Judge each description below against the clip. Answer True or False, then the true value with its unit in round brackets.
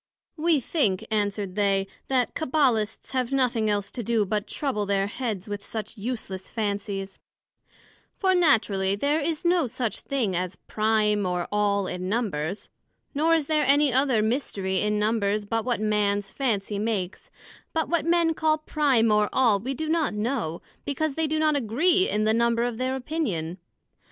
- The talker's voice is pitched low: False (225 Hz)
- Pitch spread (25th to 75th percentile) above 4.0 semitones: True (5.6 semitones)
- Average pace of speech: True (170 wpm)